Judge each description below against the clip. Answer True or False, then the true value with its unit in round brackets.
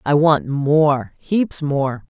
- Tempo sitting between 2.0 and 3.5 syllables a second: True (2.8 syllables/s)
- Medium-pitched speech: True (150 Hz)